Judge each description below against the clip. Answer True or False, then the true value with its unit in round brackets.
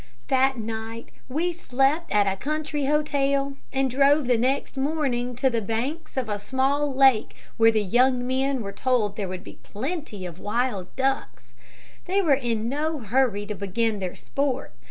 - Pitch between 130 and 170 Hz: False (255 Hz)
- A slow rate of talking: False (170 wpm)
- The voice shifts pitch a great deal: False (4.0 semitones)